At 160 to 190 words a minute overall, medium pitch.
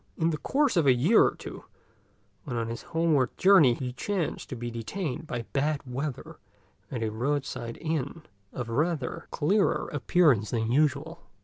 Yes: average, 165 wpm; medium, 145 Hz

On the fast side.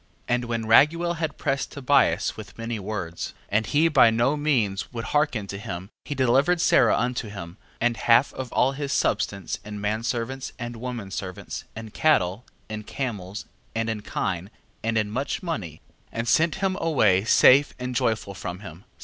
No: average, 175 wpm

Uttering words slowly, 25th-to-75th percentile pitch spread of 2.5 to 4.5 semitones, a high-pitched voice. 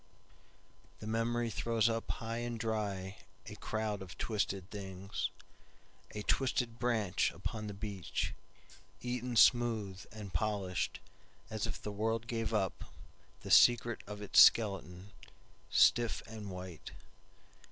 No: slow, 100 wpm; average, 2.8 semitones; low, 110 Hz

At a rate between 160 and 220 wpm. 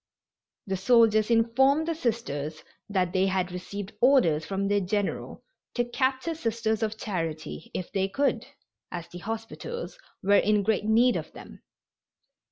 No: average, 145 wpm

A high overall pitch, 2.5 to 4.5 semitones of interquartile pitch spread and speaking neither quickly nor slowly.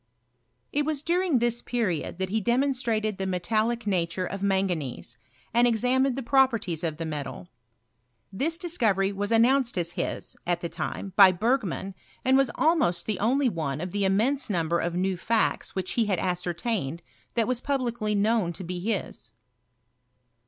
No: high, 210 Hz; wide, 5.4 semitones; average, 165 wpm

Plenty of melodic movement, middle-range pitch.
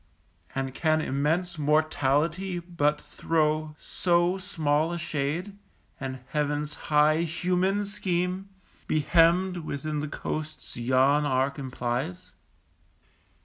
No: average, 3.2 semitones; medium, 155 Hz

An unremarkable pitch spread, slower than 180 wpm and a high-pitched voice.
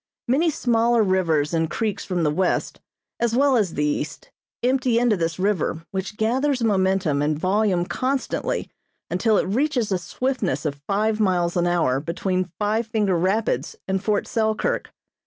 Yes: average, 4.7 semitones; average, 155 wpm; high, 200 Hz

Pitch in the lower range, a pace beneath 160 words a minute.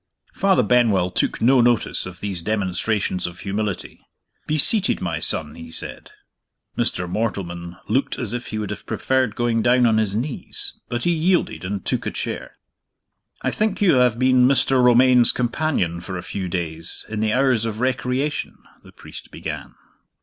No: low, 115 Hz; average, 170 wpm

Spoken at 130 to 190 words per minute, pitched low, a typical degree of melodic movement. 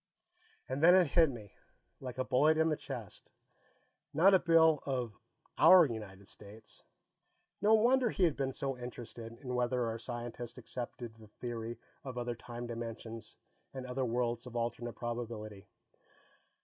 Yes: average, 150 wpm; low, 120 Hz; average, 3.2 semitones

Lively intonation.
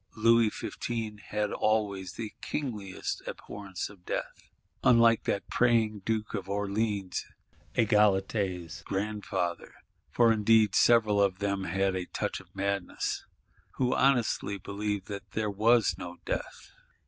No: narrow, 2.4 semitones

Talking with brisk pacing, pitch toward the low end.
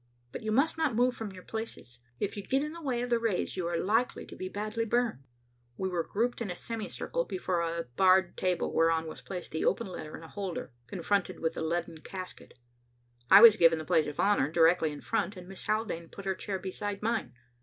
No: fast, 230 wpm; high, 190 Hz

